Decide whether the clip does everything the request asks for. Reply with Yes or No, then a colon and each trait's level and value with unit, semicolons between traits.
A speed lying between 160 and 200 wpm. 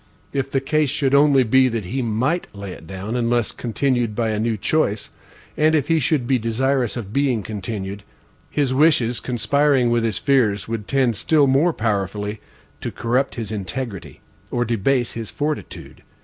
Yes: average, 170 wpm